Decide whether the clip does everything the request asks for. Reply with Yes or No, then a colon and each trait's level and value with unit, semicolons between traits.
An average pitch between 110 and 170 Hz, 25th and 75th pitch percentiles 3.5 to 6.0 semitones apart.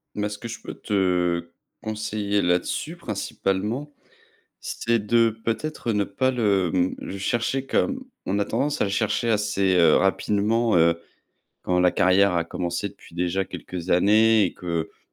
No: low, 100 Hz; average, 3.8 semitones